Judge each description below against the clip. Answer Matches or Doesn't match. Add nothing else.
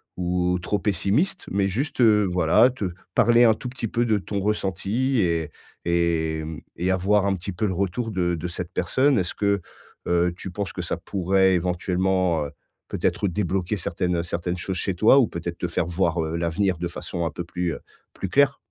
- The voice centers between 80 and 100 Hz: Matches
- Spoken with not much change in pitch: Doesn't match